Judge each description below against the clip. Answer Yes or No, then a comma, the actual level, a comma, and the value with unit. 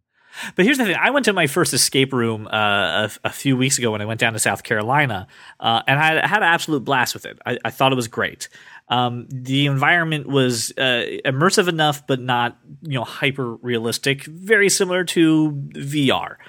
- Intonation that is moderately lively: Yes, average, 4.6 semitones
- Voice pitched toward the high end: No, low, 135 Hz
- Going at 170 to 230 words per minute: Yes, fast, 205 wpm